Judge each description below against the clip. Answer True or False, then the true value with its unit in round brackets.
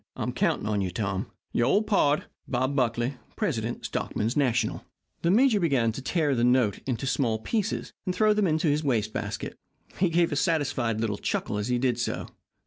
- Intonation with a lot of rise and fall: True (6.1 semitones)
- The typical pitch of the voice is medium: False (130 Hz)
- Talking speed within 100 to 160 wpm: False (190 wpm)